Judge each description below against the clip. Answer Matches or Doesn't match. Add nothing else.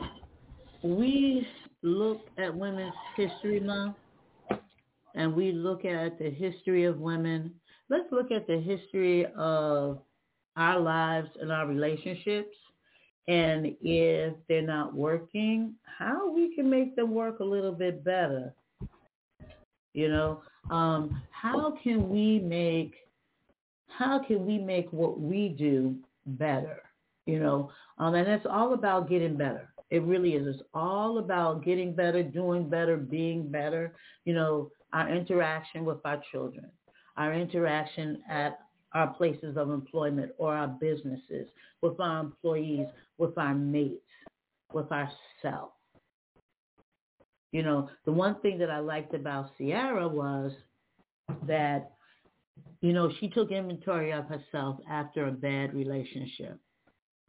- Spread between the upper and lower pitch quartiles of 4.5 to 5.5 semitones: Doesn't match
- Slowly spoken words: Matches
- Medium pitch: Matches